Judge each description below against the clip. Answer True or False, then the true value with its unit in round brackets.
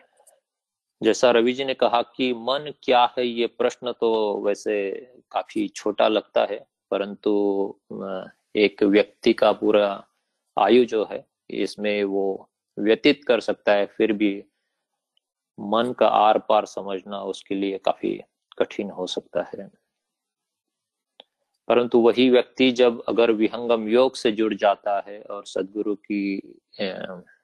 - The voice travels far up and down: False (3.1 semitones)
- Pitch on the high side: False (110 Hz)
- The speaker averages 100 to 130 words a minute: True (125 wpm)